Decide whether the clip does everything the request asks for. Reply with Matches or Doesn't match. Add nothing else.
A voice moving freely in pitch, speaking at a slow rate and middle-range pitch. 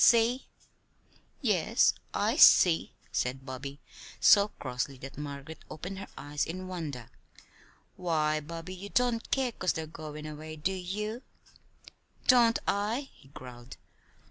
Matches